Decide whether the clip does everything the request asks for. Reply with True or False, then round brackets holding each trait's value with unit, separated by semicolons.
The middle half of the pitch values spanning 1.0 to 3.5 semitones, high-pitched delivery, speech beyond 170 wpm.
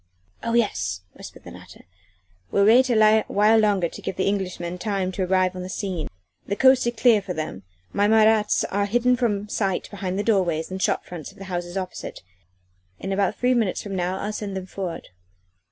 True (2.8 semitones; 200 Hz; 195 wpm)